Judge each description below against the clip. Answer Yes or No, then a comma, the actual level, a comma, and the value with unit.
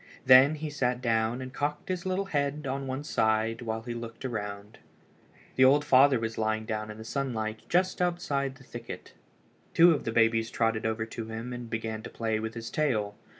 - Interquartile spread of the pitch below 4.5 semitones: Yes, average, 3.8 semitones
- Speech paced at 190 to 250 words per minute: Yes, average, 195 wpm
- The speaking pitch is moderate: No, low, 120 Hz